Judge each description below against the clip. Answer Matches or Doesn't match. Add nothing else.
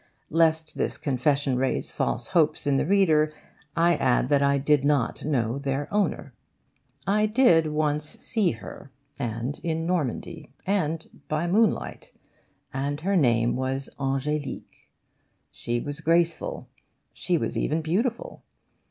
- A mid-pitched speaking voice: Matches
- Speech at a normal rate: Doesn't match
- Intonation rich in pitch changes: Doesn't match